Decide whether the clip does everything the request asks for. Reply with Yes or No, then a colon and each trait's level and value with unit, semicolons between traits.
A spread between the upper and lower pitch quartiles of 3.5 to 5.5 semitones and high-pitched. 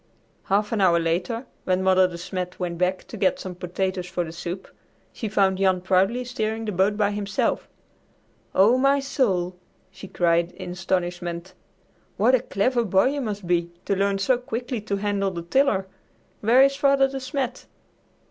Yes: average, 4.3 semitones; high, 195 Hz